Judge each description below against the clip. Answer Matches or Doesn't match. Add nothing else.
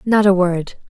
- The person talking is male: Doesn't match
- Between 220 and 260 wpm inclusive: Doesn't match